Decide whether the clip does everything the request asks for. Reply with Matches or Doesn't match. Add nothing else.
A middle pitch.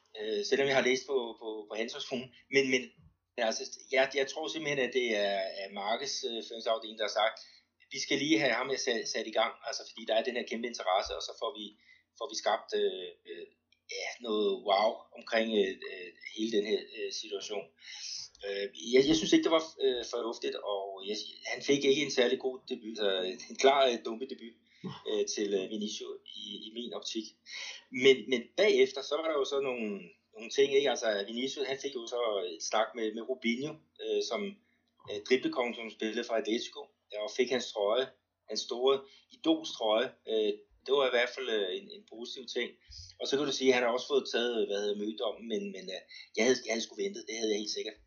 Matches